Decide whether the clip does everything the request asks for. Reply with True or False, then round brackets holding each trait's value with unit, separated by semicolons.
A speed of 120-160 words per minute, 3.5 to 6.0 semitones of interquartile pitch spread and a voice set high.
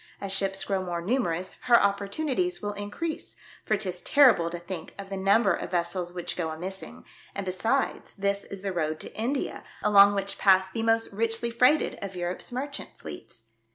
False (190 wpm; 3.8 semitones; 200 Hz)